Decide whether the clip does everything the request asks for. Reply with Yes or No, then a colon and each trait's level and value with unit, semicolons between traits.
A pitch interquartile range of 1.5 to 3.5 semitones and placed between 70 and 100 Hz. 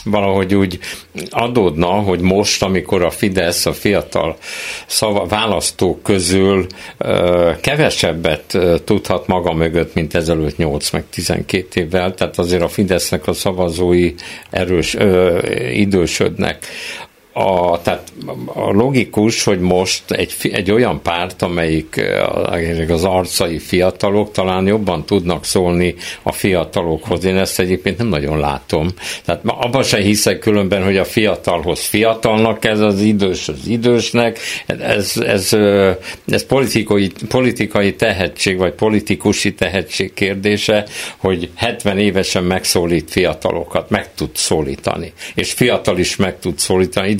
Yes: average, 2.9 semitones; very low, 95 Hz